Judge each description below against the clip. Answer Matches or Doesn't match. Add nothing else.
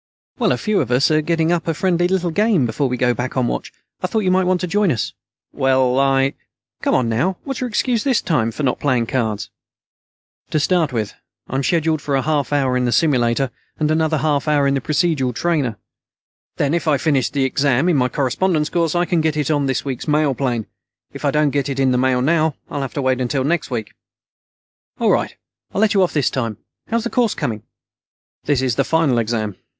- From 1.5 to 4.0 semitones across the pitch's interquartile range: Doesn't match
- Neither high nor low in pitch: Matches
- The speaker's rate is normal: Doesn't match